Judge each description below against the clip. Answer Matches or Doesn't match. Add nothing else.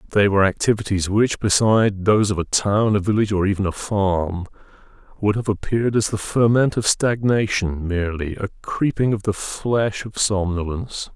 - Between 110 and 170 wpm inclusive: Matches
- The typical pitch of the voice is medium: Doesn't match